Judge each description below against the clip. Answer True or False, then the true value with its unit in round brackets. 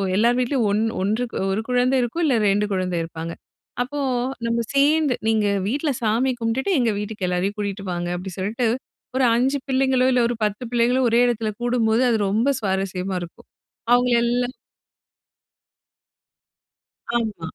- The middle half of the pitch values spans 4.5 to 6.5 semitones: False (3.8 semitones)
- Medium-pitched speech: False (230 Hz)